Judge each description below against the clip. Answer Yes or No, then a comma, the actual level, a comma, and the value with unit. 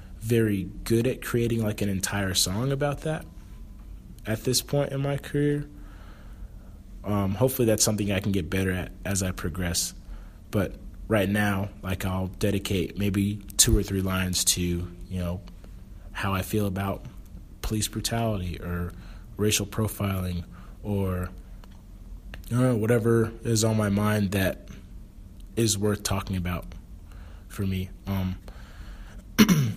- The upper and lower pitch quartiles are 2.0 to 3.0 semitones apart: Yes, narrow, 2.5 semitones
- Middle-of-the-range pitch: No, low, 100 Hz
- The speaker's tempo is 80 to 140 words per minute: Yes, slow, 135 wpm